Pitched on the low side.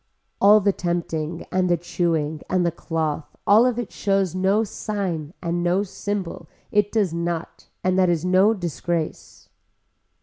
No: medium, 180 Hz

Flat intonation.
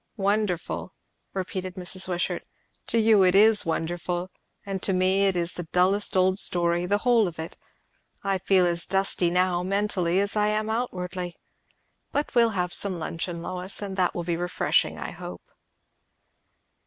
Yes: narrow, 2.2 semitones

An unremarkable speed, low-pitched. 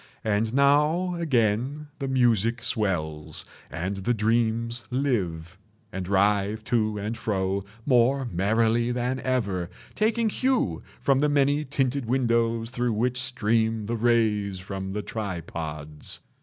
No: slow, 125 wpm; low, 115 Hz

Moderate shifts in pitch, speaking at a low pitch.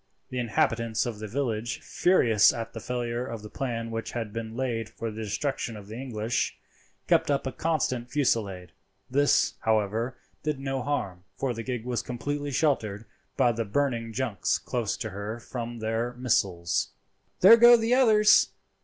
Yes: average, 3.3 semitones; low, 120 Hz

